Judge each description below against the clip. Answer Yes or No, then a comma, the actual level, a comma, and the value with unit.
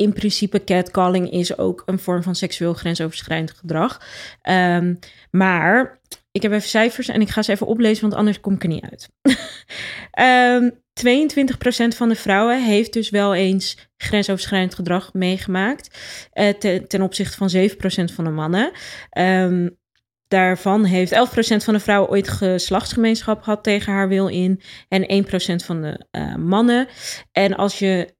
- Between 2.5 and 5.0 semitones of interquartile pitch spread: Yes, average, 2.9 semitones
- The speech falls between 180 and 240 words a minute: No, average, 155 wpm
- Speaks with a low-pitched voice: No, high, 195 Hz